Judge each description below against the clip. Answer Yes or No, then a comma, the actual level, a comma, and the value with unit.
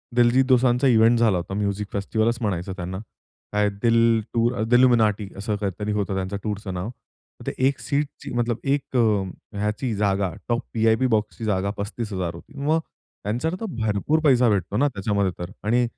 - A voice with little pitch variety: No, average, 3.2 semitones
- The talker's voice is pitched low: Yes, low, 110 Hz